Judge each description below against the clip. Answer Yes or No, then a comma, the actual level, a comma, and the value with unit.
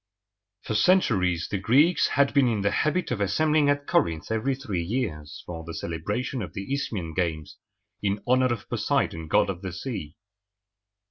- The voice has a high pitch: No, low, 105 Hz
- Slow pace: No, average, 165 wpm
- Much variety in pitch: Yes, wide, 7.5 semitones